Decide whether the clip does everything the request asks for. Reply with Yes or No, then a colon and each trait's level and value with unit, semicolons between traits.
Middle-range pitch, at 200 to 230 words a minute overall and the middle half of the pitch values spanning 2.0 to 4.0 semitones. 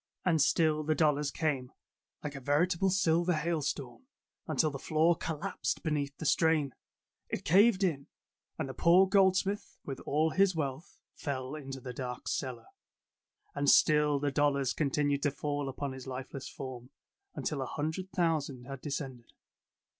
No: medium, 150 Hz; average, 155 wpm; average, 3.2 semitones